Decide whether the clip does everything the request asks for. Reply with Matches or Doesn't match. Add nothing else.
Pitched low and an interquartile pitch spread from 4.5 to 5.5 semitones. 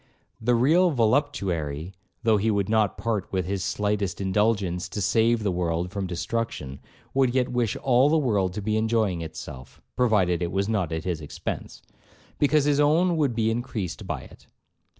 Matches